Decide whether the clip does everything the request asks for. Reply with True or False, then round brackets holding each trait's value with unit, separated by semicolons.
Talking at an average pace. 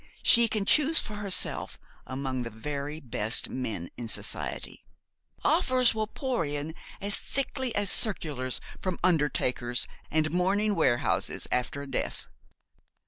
False (130 wpm)